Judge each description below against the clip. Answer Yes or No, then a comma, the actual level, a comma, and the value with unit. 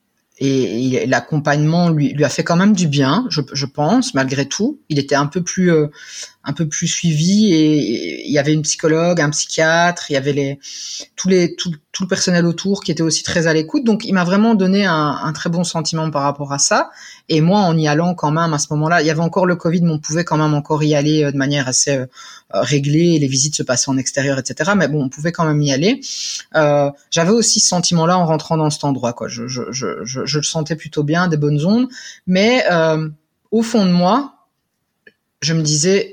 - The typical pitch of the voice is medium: Yes, medium, 160 Hz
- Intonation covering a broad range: No, average, 3.4 semitones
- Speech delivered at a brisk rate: Yes, fast, 235 wpm